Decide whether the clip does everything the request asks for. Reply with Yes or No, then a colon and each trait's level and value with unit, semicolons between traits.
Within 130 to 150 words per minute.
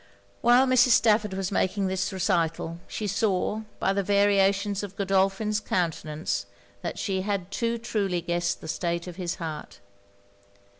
Yes: average, 145 wpm